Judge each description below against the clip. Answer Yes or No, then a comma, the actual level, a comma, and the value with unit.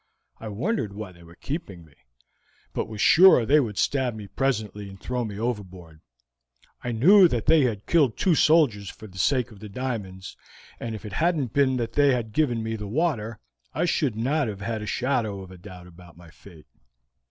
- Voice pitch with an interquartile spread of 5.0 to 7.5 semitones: Yes, wide, 5.4 semitones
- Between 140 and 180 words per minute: No, average, 200 wpm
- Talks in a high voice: No, low, 110 Hz